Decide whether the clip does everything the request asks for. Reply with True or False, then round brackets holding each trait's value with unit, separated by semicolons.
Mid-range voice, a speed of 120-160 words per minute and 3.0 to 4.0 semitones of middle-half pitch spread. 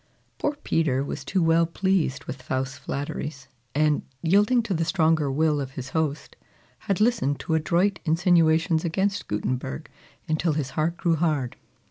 True (160 Hz; 150 wpm; 3.7 semitones)